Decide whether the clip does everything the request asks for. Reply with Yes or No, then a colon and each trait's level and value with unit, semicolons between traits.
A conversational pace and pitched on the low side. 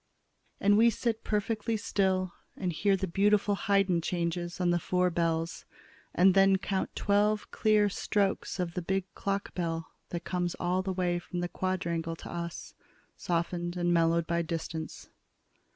No: average, 160 wpm; medium, 180 Hz